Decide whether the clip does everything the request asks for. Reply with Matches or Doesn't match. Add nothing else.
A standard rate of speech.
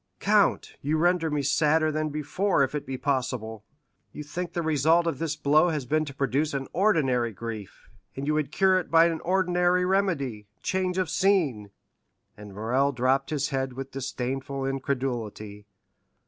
Matches